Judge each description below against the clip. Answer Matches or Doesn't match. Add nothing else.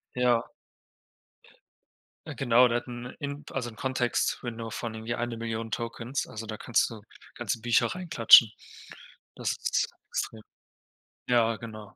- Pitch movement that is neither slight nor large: Doesn't match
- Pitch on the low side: Matches